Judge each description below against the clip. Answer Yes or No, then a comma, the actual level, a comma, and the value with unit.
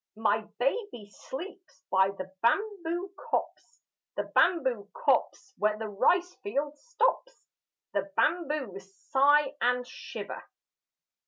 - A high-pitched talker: Yes, very high, 275 Hz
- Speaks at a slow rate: Yes, slow, 105 wpm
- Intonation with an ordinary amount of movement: No, wide, 8.8 semitones